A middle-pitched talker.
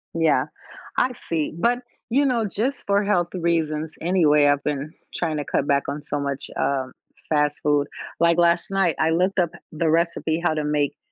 Yes: medium, 160 Hz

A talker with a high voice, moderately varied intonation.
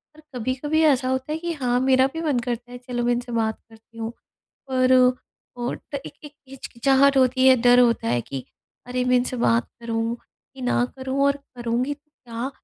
No: very high, 250 Hz; narrow, 2.0 semitones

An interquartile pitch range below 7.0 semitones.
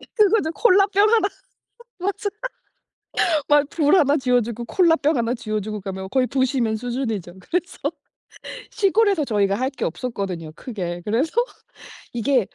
No: wide, 7.8 semitones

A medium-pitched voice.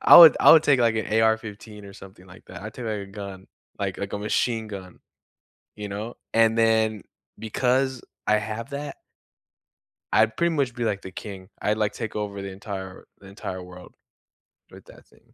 No: low, 105 Hz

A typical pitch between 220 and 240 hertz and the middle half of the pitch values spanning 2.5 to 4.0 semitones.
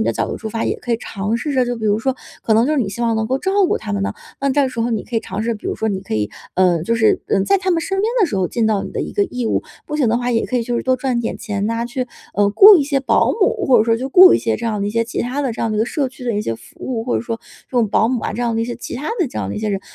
Yes: high, 235 Hz; average, 3.4 semitones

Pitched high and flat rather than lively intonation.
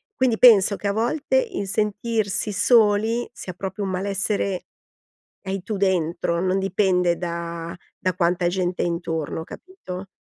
No: high, 195 Hz; average, 3.1 semitones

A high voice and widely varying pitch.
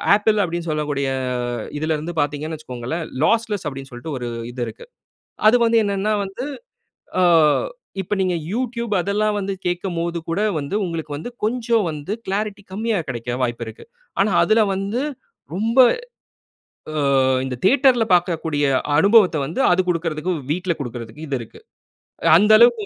No: medium, 180 Hz; wide, 5.8 semitones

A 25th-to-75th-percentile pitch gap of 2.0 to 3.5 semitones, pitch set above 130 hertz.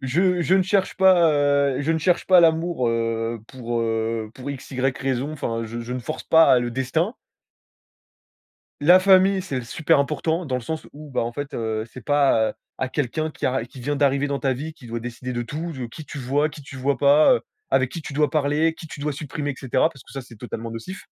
No: average, 4.3 semitones; medium, 140 Hz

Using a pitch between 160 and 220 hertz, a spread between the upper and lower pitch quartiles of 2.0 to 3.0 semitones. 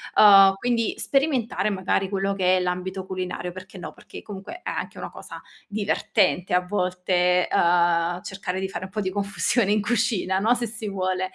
Yes: high, 190 Hz; narrow, 2.3 semitones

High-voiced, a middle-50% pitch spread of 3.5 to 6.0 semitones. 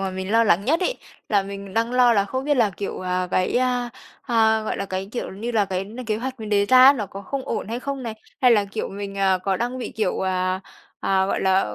Yes: high, 210 Hz; average, 4.1 semitones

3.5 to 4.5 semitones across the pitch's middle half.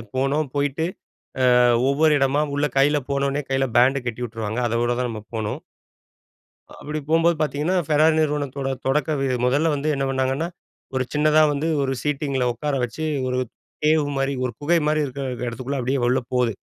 No: average, 2.8 semitones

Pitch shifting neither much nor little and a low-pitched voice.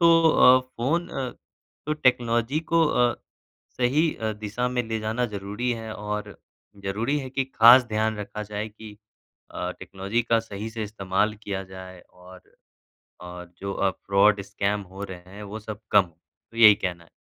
Yes: average, 3.7 semitones; low, 110 Hz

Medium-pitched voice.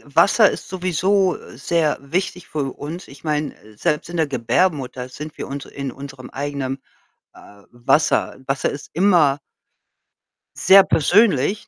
Yes: medium, 150 Hz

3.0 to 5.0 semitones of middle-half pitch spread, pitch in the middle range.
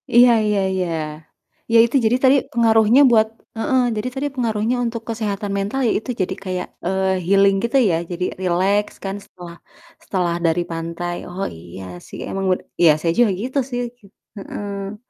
No: average, 4.2 semitones; high, 200 Hz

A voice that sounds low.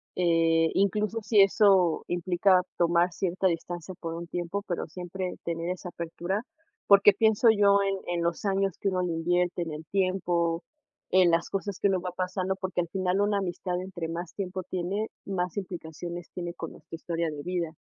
No: medium, 180 Hz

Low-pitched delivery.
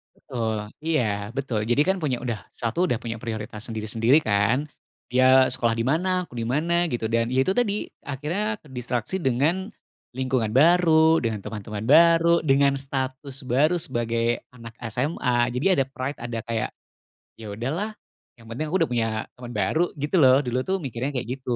Yes: low, 130 Hz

